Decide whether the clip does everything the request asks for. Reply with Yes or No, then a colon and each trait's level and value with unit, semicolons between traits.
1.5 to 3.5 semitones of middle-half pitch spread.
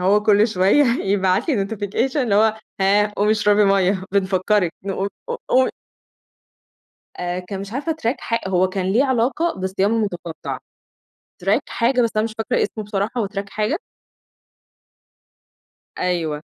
Yes: average, 3.0 semitones